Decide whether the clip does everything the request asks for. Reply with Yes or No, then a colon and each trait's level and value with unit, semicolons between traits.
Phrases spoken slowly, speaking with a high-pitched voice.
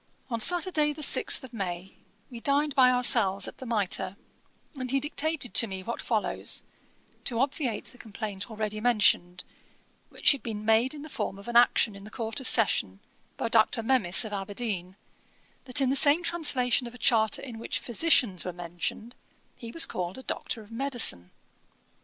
No: average, 175 wpm; high, 230 Hz